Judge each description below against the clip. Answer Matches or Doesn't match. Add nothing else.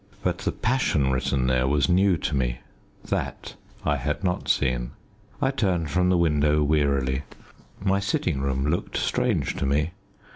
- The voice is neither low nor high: Doesn't match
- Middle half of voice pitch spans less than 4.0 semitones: Doesn't match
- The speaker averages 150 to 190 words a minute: Matches